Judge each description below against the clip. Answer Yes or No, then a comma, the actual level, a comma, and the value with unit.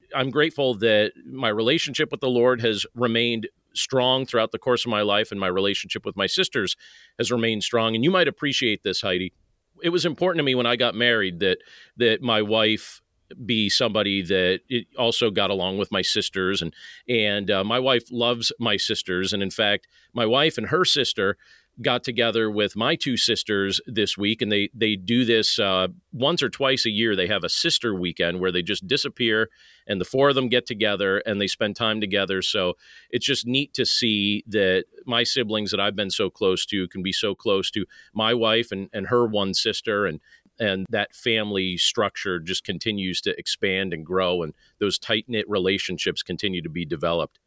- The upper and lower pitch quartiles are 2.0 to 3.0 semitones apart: No, average, 3.7 semitones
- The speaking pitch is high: No, low, 110 Hz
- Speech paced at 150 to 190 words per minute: No, average, 200 wpm